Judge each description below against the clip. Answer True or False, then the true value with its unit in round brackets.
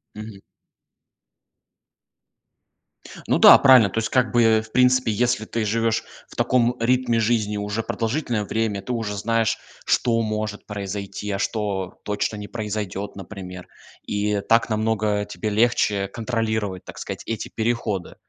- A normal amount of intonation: False (2.0 semitones)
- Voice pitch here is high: False (110 Hz)